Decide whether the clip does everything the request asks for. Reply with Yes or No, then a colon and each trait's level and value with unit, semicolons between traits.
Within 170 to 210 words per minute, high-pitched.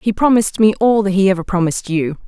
No: fast, 235 wpm; high, 195 Hz